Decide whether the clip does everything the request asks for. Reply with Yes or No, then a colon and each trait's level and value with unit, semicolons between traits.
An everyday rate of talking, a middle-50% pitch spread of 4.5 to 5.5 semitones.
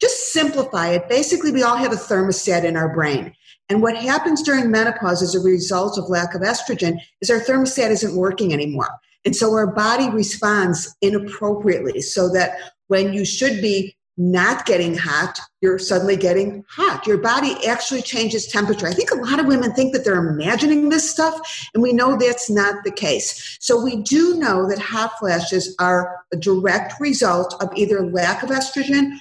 Yes: average, 185 wpm; average, 5.2 semitones